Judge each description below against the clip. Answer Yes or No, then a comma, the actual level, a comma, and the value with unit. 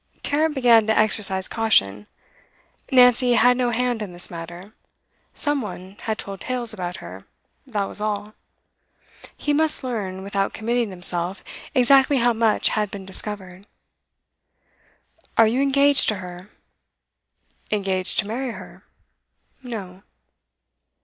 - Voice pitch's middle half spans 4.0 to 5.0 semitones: Yes, average, 4.5 semitones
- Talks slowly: Yes, slow, 125 wpm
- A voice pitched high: Yes, high, 215 Hz